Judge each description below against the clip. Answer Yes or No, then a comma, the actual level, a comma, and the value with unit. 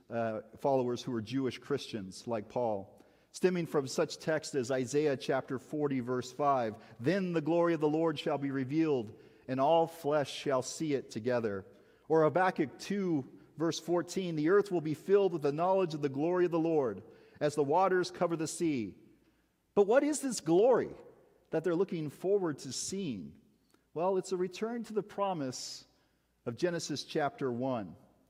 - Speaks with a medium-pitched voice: Yes, medium, 155 Hz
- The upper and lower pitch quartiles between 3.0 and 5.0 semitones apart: No, wide, 5.4 semitones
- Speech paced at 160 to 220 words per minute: Yes, average, 170 wpm